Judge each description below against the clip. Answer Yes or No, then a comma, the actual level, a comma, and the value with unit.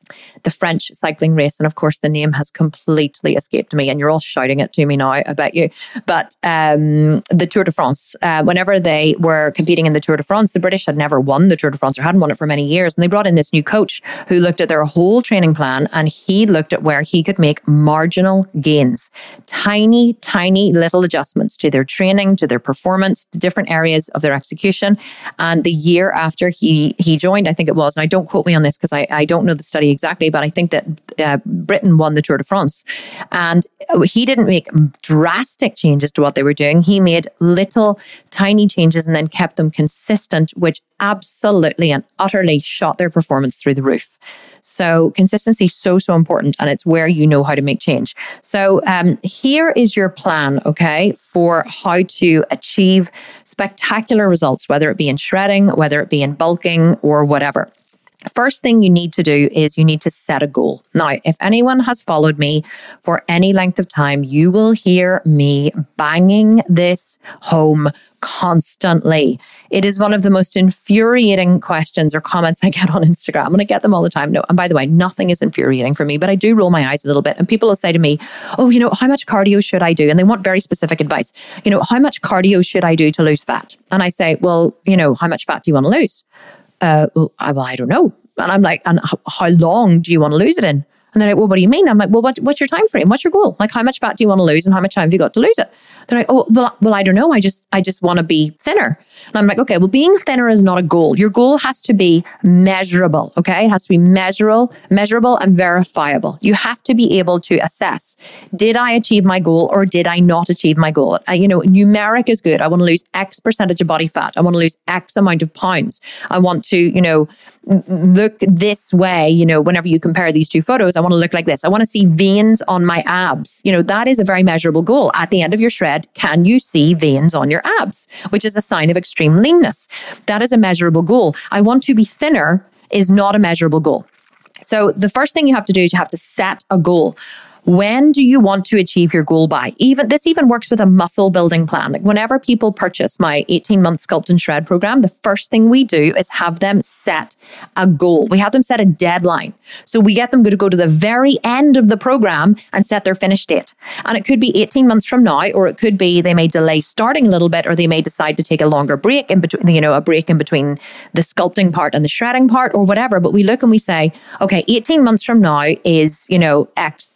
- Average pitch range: Yes, average, 4.4 semitones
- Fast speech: Yes, fast, 245 wpm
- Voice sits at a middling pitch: Yes, medium, 180 Hz